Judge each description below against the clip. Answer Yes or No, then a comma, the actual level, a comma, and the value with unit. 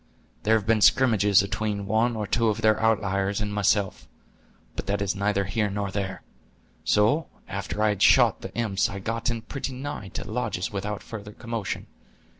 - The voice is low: Yes, low, 105 Hz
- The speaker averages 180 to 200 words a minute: Yes, average, 185 wpm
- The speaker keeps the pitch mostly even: Yes, narrow, 2.1 semitones